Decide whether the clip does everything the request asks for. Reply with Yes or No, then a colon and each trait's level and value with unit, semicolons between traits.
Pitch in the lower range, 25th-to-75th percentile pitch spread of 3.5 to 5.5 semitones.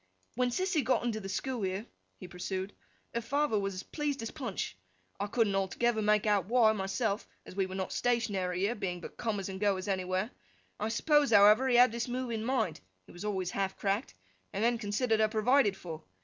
No: high, 210 Hz; average, 3.9 semitones